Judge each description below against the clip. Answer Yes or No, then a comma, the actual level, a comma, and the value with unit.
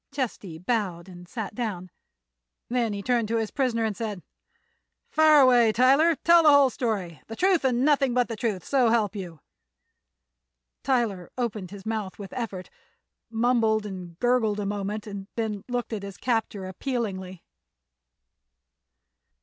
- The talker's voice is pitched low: No, high, 220 Hz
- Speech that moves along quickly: No, average, 145 wpm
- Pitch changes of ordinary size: Yes, average, 4.0 semitones